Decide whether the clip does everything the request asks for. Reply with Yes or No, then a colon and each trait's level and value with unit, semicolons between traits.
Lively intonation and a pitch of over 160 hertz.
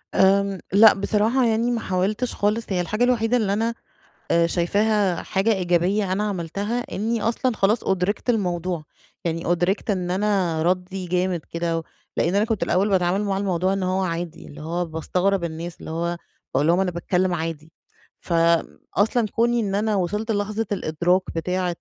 No: average, 3.4 semitones; high, 190 Hz